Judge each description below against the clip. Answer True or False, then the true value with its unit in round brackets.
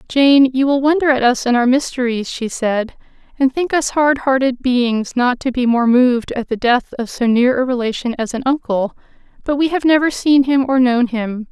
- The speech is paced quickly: True (220 wpm)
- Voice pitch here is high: True (255 Hz)